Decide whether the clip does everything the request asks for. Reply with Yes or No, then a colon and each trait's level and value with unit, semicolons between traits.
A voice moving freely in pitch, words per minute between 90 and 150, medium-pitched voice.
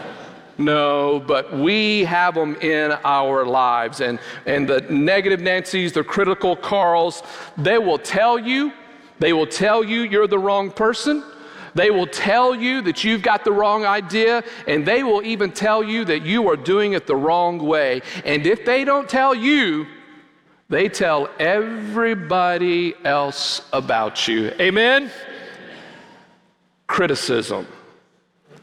No: wide, 6.5 semitones; average, 140 wpm; high, 200 Hz